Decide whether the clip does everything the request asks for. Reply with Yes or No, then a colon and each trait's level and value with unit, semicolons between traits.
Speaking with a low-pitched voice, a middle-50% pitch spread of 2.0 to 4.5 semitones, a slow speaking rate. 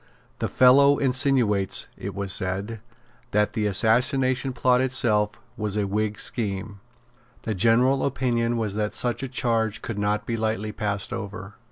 No: low, 110 Hz; average, 3.2 semitones; average, 150 wpm